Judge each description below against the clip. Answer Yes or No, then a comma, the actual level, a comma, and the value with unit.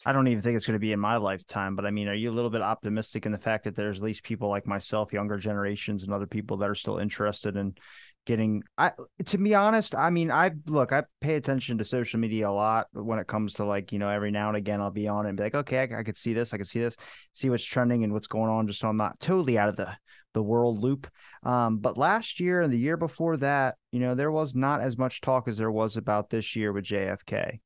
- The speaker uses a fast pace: Yes, fast, 280 wpm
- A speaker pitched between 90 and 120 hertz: Yes, low, 110 Hz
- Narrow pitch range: No, average, 3.6 semitones